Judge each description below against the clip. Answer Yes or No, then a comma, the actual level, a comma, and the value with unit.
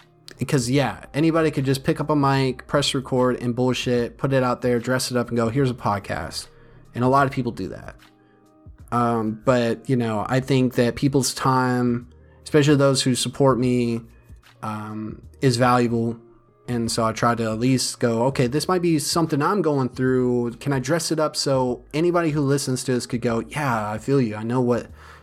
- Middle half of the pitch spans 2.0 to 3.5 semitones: Yes, average, 2.9 semitones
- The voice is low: Yes, low, 125 Hz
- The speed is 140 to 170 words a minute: No, average, 200 wpm